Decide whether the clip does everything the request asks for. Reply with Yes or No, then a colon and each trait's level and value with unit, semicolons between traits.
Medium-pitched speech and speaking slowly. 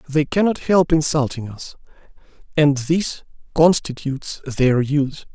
Yes: medium, 145 Hz; slow, 110 wpm